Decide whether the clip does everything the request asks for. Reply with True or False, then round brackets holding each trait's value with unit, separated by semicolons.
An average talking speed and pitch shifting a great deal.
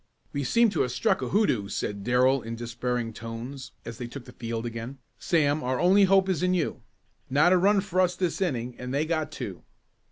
False (215 wpm; 7.0 semitones)